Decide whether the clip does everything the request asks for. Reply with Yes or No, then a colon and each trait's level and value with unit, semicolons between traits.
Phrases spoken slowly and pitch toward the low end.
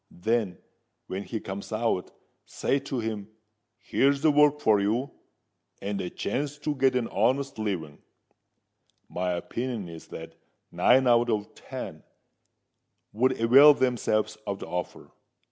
Yes: slow, 130 wpm; low, 115 Hz